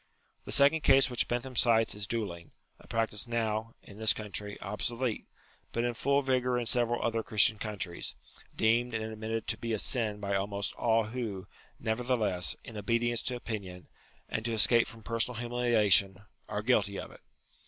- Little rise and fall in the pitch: Yes, narrow, 2.3 semitones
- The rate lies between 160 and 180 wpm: Yes, average, 170 wpm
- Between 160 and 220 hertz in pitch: No, low, 115 Hz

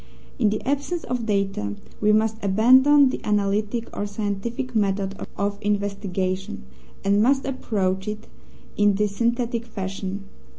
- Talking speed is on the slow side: Yes, slow, 130 wpm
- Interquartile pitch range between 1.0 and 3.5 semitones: Yes, average, 3.0 semitones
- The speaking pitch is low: No, high, 210 Hz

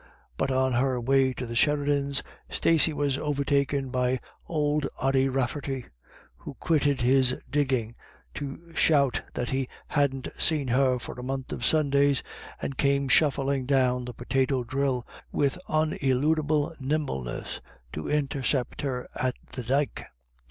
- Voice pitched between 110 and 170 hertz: Yes, low, 135 Hz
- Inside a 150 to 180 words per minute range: No, slow, 135 wpm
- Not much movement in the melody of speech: Yes, narrow, 2.1 semitones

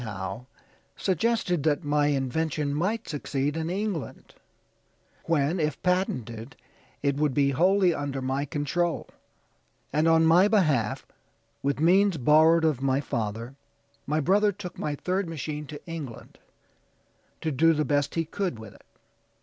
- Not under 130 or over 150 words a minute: Yes, average, 140 wpm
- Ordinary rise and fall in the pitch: Yes, average, 3.8 semitones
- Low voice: No, medium, 150 Hz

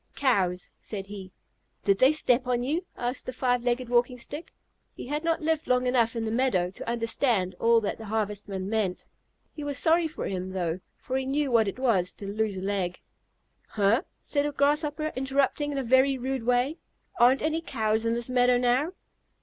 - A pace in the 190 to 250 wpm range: Yes, average, 195 wpm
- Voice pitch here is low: No, high, 245 Hz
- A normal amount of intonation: Yes, average, 4.5 semitones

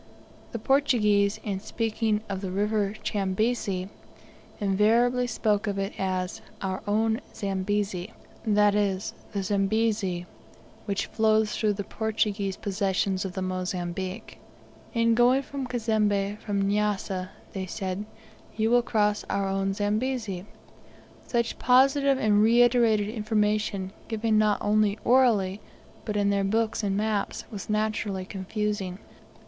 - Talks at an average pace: No, slow, 125 wpm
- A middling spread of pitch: No, narrow, 2.2 semitones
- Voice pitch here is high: Yes, high, 210 Hz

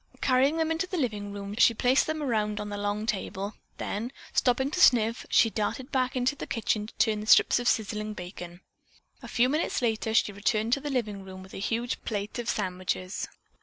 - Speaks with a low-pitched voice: No, high, 220 Hz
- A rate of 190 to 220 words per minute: Yes, fast, 205 wpm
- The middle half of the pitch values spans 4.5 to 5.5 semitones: No, average, 3.7 semitones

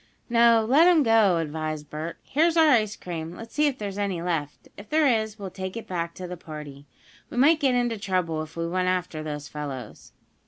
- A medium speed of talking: No, fast, 210 wpm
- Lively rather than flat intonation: Yes, wide, 6.4 semitones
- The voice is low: No, medium, 185 Hz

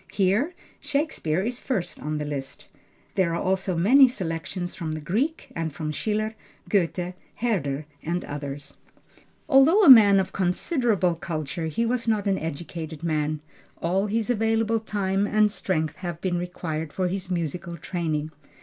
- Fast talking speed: No, average, 150 wpm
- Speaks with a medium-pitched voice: Yes, medium, 180 Hz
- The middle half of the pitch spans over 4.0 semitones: Yes, average, 5.1 semitones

